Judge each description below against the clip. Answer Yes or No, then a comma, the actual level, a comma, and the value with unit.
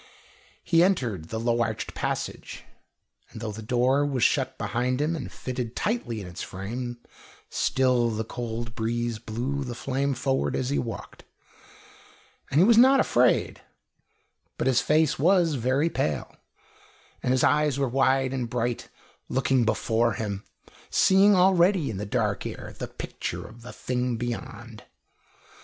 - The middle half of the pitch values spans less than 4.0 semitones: Yes, average, 3.4 semitones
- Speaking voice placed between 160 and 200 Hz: No, low, 125 Hz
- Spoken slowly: No, average, 150 wpm